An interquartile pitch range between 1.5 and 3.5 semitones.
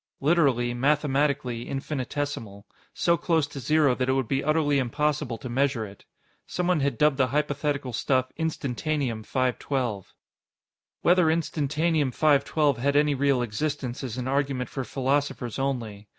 Yes: average, 3.0 semitones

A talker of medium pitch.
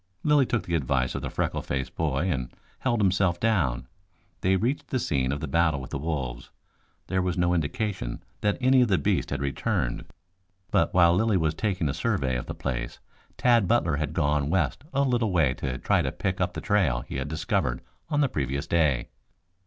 No: very low, 85 Hz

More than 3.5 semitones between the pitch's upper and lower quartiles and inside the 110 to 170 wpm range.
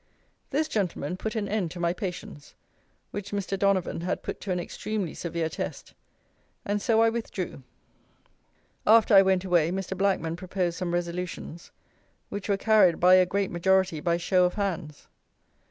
No: narrow, 2.6 semitones; average, 160 wpm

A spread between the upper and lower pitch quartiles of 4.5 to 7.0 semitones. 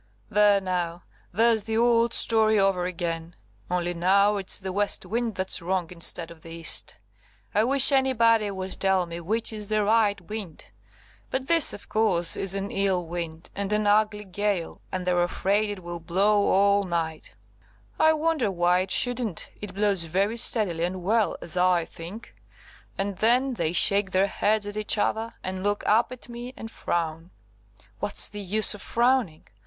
No: average, 3.5 semitones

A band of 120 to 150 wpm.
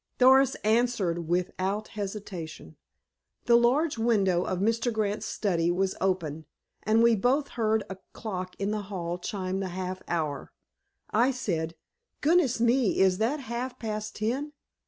Yes: average, 140 wpm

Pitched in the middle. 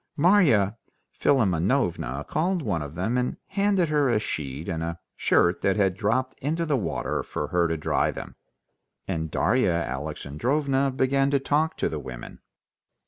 No: low, 110 Hz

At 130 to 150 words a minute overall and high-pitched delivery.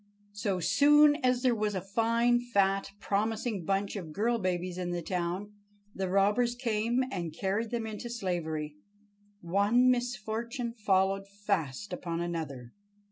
Yes: slow, 135 wpm; high, 205 Hz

